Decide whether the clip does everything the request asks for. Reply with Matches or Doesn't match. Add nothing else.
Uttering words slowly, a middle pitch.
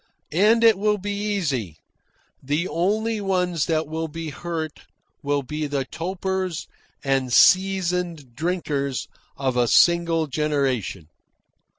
Matches